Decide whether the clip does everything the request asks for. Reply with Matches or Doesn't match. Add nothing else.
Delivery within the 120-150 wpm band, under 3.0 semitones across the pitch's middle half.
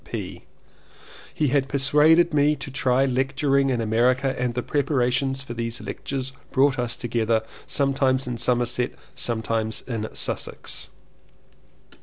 Matches